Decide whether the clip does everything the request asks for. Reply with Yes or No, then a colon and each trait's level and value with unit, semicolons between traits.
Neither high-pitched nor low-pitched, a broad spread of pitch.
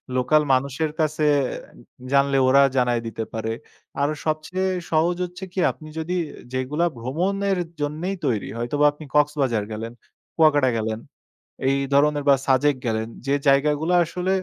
No: medium, 145 Hz; average, 3.6 semitones